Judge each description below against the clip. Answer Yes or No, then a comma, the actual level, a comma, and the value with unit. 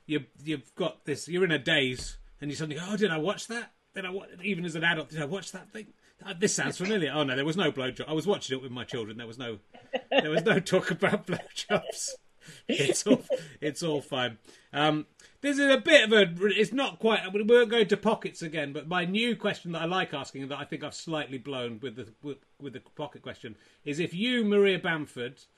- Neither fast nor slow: No, fast, 240 wpm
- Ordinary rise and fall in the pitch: No, wide, 6.3 semitones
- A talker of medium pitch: Yes, medium, 165 Hz